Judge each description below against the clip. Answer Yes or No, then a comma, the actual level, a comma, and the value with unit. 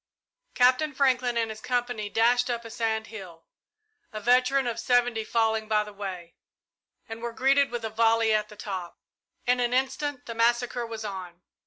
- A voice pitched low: No, high, 230 Hz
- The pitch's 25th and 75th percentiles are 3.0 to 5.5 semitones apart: No, narrow, 2.4 semitones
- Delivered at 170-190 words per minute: Yes, average, 175 wpm